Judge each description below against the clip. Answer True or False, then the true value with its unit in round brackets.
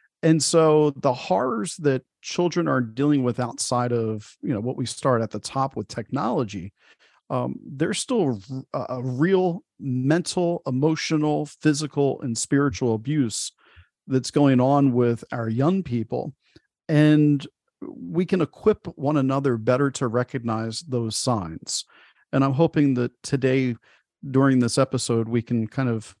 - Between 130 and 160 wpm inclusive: True (140 wpm)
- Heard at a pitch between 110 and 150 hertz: True (135 Hz)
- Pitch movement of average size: True (3.8 semitones)